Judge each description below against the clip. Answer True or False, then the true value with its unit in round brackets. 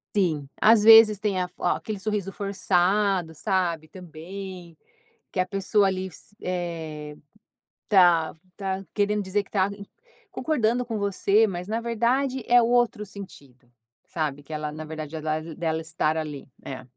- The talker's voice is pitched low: False (190 Hz)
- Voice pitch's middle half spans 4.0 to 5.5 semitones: True (4.6 semitones)